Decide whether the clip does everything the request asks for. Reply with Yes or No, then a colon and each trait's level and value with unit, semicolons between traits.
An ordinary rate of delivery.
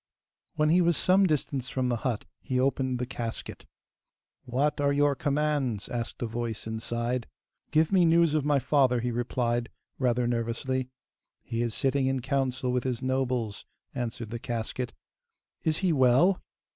Yes: average, 160 wpm